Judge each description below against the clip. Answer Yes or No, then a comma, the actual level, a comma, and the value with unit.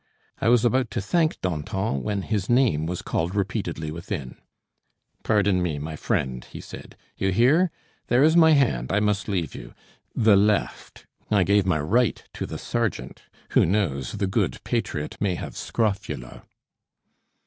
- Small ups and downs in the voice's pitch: No, wide, 5.6 semitones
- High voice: No, low, 100 Hz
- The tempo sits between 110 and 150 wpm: No, average, 160 wpm